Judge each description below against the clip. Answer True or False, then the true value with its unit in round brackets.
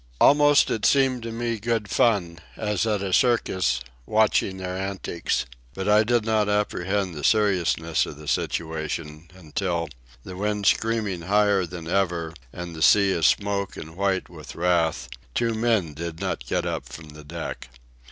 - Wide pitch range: False (4.1 semitones)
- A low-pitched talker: True (95 Hz)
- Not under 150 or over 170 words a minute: True (160 wpm)